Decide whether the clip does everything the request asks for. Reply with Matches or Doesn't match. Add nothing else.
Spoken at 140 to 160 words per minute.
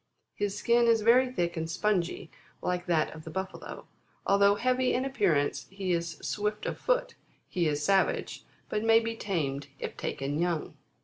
Doesn't match